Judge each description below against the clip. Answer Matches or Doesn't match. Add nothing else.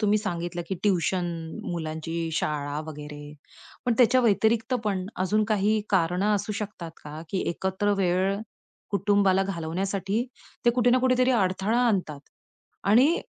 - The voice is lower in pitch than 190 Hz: Doesn't match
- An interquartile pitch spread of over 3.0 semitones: Matches